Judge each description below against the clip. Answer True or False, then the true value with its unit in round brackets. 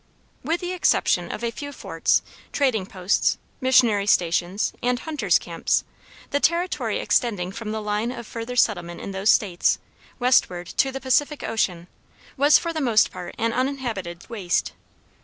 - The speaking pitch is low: False (230 Hz)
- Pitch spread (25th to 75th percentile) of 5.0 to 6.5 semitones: True (5.6 semitones)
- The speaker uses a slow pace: False (155 wpm)